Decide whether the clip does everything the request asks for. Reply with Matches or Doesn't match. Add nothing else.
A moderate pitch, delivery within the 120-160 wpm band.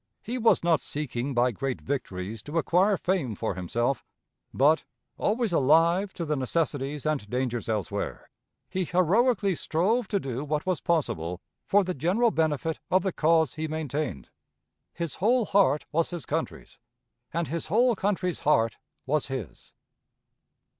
Matches